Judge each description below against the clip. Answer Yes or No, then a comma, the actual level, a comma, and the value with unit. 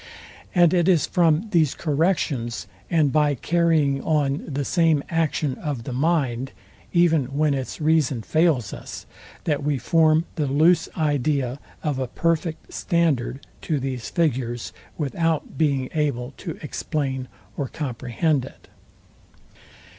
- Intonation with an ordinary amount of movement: Yes, average, 3.5 semitones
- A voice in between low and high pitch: Yes, medium, 150 Hz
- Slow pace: Yes, slow, 130 wpm